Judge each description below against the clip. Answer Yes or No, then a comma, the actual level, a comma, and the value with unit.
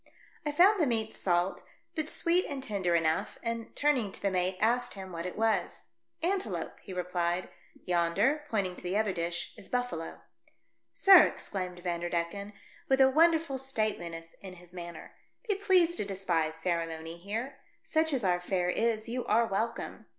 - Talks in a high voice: Yes, high, 200 Hz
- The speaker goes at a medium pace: Yes, average, 170 wpm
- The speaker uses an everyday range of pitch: No, wide, 7.0 semitones